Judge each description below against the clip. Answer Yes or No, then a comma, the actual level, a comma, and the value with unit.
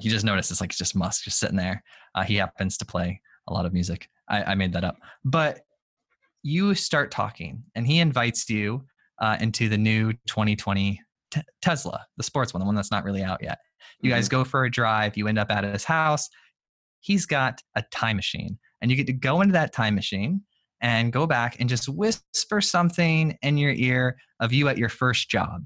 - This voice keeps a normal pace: No, fast, 215 wpm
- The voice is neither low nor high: No, low, 120 Hz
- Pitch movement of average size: No, wide, 6.1 semitones